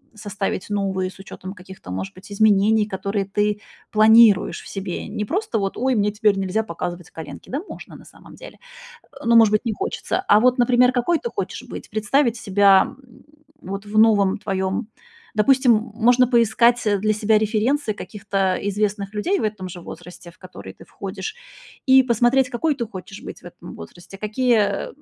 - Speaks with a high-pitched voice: Yes, high, 210 Hz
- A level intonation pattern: No, average, 3.2 semitones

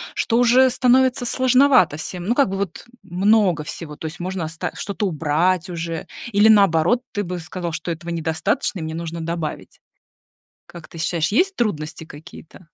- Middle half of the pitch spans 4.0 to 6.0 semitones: Yes, average, 5.1 semitones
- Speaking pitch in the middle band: Yes, medium, 175 Hz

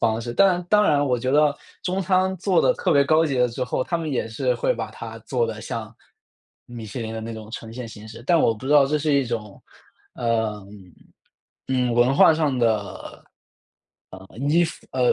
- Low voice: Yes, low, 125 Hz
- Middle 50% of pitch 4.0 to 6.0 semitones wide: Yes, average, 4.7 semitones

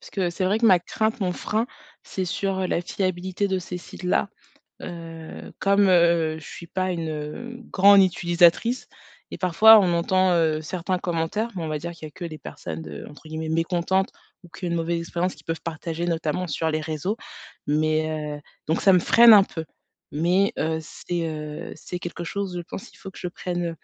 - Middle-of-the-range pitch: Yes, medium, 175 Hz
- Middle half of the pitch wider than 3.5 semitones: No, average, 2.8 semitones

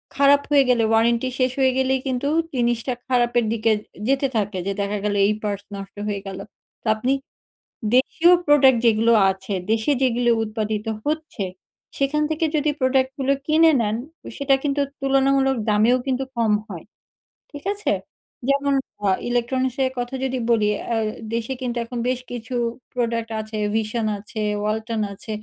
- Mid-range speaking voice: No, high, 245 Hz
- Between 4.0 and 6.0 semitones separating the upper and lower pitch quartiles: No, average, 3.5 semitones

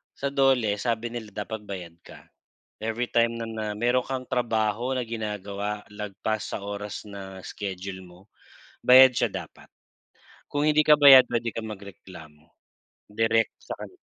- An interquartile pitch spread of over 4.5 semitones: No, average, 3.2 semitones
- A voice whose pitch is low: Yes, low, 110 Hz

